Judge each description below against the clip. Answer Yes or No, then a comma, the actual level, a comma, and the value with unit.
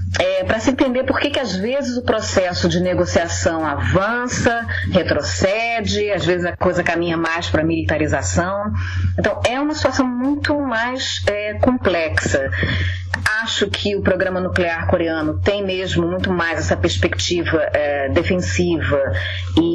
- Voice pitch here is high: No, medium, 175 Hz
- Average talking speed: Yes, average, 140 wpm